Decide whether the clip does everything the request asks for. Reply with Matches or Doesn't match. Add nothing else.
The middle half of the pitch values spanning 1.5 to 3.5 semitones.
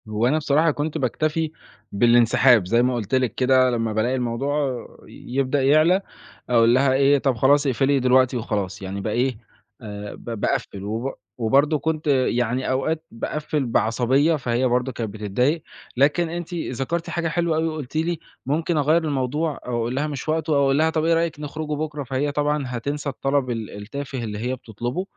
Doesn't match